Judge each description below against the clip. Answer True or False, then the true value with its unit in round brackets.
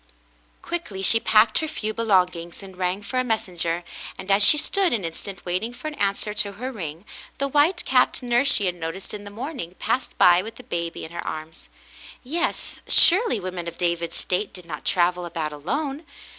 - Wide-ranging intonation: True (6.2 semitones)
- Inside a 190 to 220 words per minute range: True (200 wpm)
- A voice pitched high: True (200 Hz)